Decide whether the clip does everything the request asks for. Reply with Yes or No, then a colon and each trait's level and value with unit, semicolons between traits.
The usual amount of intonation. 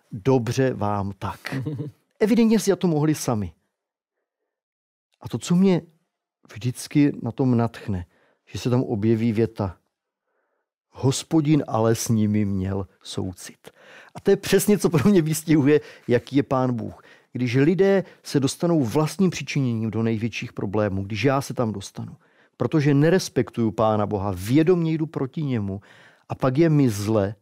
No: wide, 5.7 semitones